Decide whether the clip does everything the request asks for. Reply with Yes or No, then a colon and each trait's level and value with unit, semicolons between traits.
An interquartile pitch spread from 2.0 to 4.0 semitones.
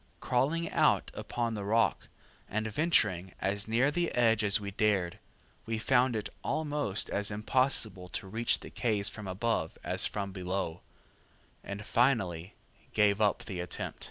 Yes: average, 3.4 semitones